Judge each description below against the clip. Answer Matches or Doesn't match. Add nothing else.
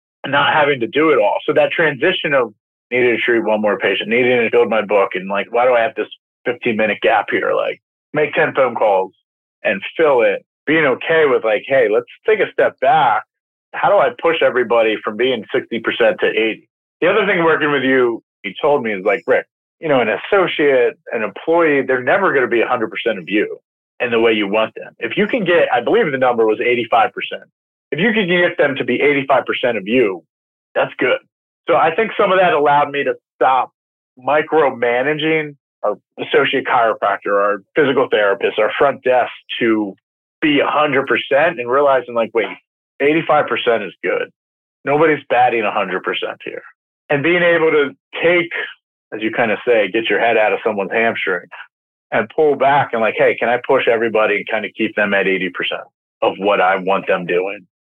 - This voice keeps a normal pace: Matches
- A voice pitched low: Doesn't match